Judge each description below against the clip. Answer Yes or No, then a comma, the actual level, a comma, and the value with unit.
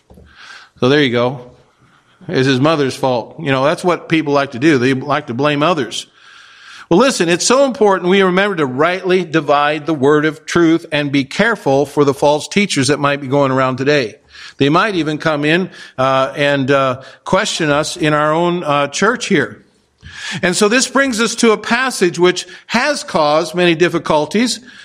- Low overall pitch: No, medium, 155 Hz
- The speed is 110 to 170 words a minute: No, average, 185 wpm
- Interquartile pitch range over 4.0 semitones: Yes, average, 4.7 semitones